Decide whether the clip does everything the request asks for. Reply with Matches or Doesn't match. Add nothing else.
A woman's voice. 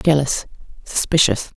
Matches